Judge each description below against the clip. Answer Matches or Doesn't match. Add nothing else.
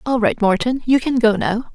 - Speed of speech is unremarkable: Doesn't match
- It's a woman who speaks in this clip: Matches